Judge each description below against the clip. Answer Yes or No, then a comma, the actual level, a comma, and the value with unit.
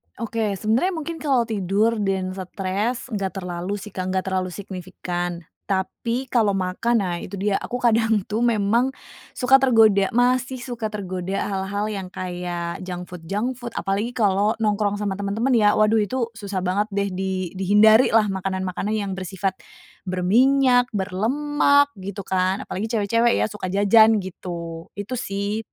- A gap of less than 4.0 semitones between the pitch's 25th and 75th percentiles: Yes, average, 3.4 semitones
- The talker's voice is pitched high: Yes, high, 205 Hz